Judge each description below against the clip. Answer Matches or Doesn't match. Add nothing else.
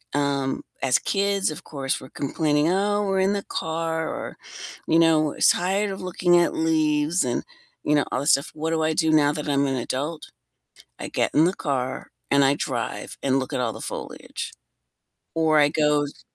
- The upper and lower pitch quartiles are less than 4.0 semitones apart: Matches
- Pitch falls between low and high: Matches